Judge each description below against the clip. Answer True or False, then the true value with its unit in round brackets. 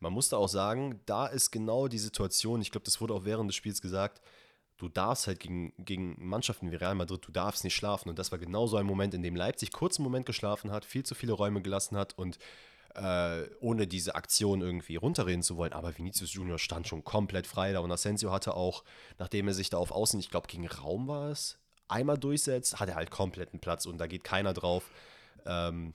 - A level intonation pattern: False (3.4 semitones)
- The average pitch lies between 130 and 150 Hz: False (95 Hz)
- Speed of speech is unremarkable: False (230 wpm)